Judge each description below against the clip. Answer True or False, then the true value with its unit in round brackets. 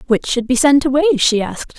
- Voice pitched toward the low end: False (260 Hz)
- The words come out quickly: True (235 wpm)